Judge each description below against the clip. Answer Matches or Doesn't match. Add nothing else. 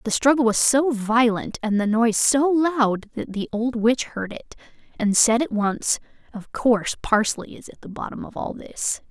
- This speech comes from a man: Doesn't match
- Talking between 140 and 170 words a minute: Doesn't match